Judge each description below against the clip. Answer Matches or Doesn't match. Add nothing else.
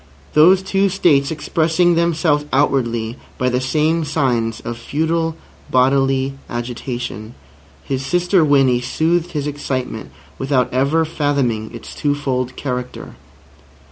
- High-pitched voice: Doesn't match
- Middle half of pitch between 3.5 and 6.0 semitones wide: Matches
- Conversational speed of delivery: Doesn't match